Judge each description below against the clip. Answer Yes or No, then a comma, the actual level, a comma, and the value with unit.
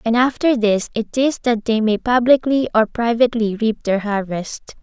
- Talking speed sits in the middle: Yes, average, 175 wpm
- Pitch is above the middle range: Yes, high, 230 Hz